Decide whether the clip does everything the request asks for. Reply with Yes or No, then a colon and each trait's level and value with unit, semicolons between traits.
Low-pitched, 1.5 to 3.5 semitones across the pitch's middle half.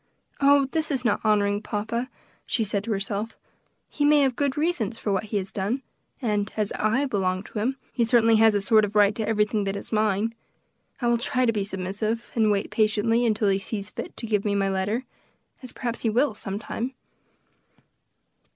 No: high, 215 Hz; average, 2.7 semitones